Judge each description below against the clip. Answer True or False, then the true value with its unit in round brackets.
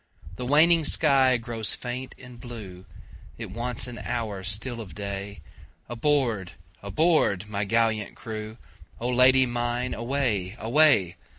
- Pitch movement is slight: False (3.8 semitones)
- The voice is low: True (115 Hz)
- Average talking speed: False (110 wpm)